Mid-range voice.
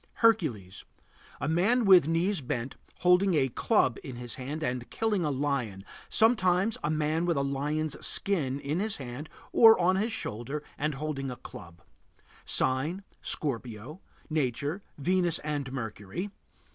Yes: medium, 150 Hz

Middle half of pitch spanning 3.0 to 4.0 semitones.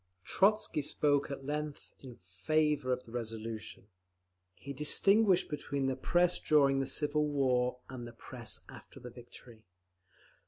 Yes: average, 3.6 semitones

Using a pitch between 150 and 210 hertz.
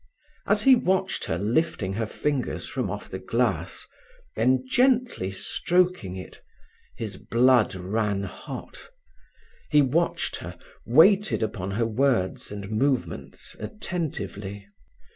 No: low, 120 Hz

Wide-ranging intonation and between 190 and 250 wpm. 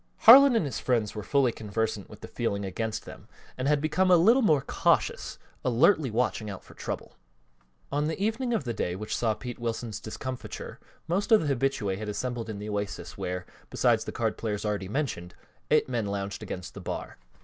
Yes: wide, 6.2 semitones; average, 195 wpm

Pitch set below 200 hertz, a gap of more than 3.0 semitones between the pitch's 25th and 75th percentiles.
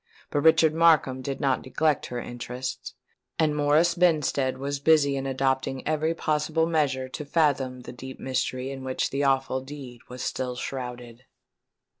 No: low, 135 Hz; average, 2.7 semitones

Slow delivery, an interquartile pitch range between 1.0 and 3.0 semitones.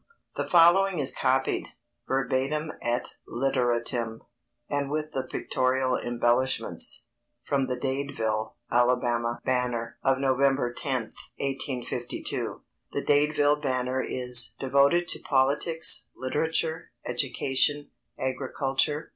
Yes: slow, 100 wpm; narrow, 2.6 semitones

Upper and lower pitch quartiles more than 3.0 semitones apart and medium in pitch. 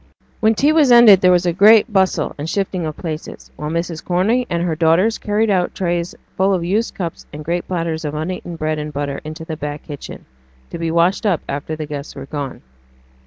Yes: average, 3.8 semitones; medium, 170 Hz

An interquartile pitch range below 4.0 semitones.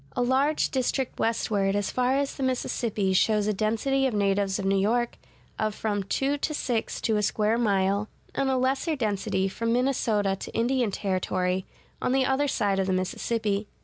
No: average, 4.6 semitones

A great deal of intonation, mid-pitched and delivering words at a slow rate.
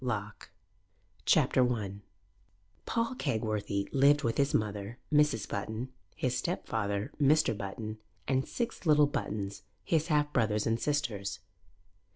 No: wide, 5.9 semitones; low, 115 Hz; slow, 120 wpm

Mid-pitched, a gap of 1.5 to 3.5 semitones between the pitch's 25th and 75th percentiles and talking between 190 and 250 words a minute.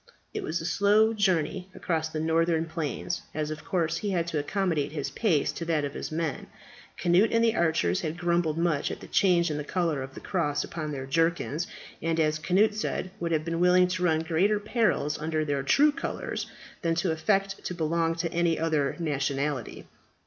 Yes: medium, 165 Hz; average, 2.8 semitones; average, 200 wpm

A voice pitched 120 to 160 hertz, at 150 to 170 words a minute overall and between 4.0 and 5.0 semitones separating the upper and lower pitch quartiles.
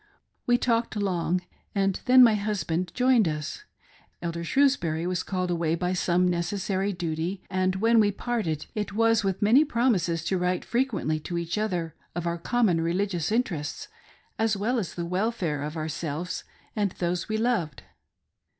No: medium, 185 Hz; average, 165 wpm; average, 4.4 semitones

